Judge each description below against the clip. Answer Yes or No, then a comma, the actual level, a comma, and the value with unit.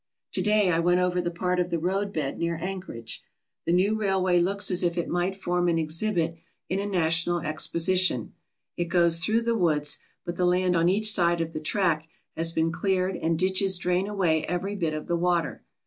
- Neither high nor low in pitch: Yes, medium, 175 Hz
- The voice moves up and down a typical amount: No, narrow, 2.1 semitones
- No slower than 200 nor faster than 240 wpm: Yes, fast, 205 wpm